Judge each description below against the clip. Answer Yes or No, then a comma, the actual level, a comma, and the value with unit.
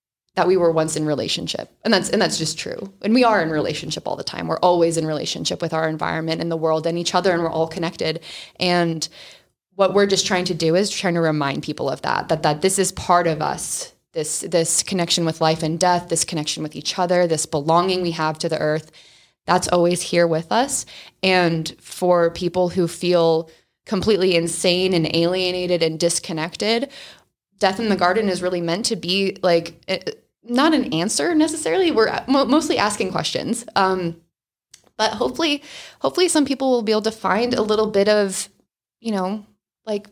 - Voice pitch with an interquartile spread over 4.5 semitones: No, average, 3.6 semitones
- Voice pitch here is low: No, medium, 180 Hz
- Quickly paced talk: No, average, 195 wpm